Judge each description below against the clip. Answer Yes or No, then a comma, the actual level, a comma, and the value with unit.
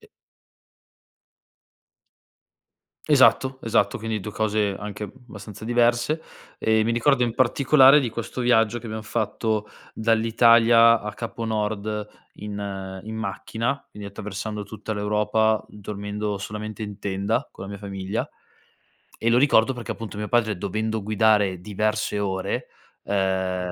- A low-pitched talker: Yes, low, 110 Hz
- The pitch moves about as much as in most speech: No, narrow, 2.1 semitones